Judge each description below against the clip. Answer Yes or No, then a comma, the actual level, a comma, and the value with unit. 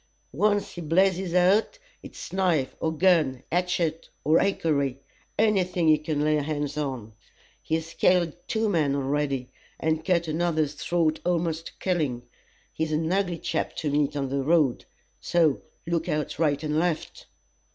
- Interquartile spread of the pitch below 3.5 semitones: Yes, average, 3.0 semitones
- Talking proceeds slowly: No, average, 150 wpm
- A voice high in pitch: No, medium, 160 Hz